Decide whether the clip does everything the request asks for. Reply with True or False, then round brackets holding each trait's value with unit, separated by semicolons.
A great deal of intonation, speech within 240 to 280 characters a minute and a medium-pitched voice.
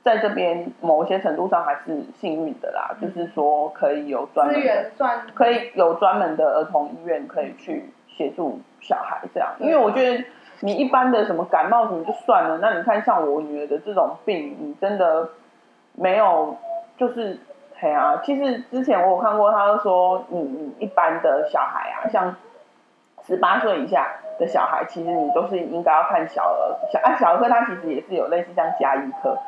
False (7.0 semitones; 270 characters per minute; 210 Hz)